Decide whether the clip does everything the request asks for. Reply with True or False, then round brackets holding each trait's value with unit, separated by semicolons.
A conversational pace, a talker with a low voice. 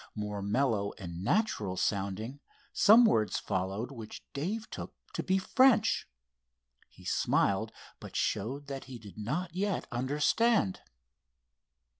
False (120 wpm; 125 Hz)